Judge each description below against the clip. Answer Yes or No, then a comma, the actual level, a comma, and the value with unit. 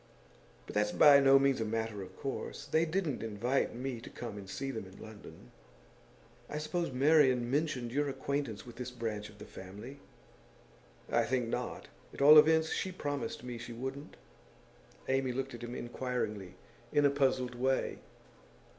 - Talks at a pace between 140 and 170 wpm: Yes, average, 165 wpm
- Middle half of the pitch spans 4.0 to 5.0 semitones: No, average, 3.6 semitones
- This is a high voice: No, low, 130 Hz